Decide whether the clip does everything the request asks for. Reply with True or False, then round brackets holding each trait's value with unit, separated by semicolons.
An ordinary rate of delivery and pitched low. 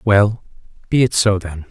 True (175 wpm; 100 Hz)